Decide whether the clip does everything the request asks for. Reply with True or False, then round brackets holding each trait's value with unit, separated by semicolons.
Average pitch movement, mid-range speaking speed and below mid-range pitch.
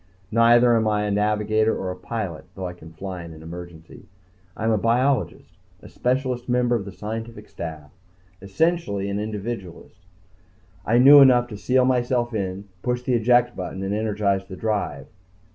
True (4.0 semitones; 170 wpm; 110 Hz)